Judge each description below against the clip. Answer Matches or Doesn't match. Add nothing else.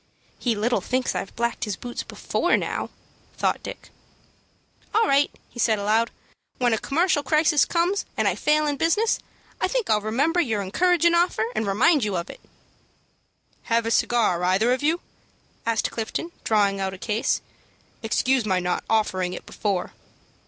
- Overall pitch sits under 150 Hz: Doesn't match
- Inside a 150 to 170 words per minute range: Matches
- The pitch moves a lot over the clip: Matches